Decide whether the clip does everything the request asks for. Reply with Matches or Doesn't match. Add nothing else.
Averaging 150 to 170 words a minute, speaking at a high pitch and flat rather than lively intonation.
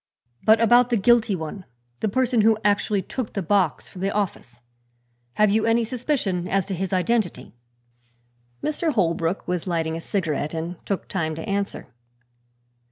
Doesn't match